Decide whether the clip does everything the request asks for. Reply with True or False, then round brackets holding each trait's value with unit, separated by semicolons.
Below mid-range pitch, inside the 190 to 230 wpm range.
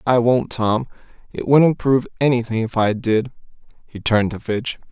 False (120 Hz; 170 wpm)